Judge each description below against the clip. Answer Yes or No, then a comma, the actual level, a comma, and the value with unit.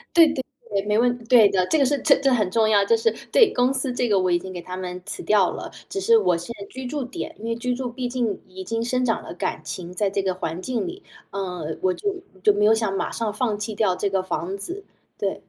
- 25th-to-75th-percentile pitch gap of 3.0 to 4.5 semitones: No, average, 4.9 semitones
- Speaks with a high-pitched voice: Yes, high, 215 Hz